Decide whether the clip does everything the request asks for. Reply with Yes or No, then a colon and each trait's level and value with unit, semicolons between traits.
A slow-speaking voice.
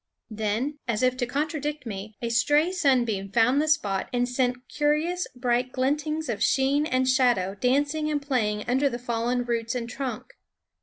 No: average, 170 wpm